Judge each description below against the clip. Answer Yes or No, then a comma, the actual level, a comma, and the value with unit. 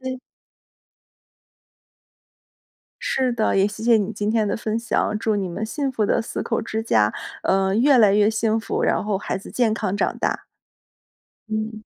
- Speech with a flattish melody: Yes, narrow, 1.9 semitones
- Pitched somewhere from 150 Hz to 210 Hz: No, high, 220 Hz